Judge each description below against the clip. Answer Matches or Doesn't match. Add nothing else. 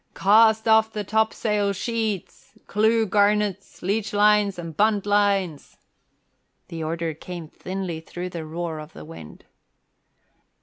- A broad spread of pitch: Doesn't match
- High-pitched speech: Matches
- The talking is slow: Matches